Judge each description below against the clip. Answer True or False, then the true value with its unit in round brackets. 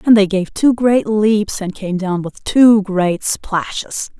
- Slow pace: False (185 wpm)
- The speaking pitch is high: True (205 Hz)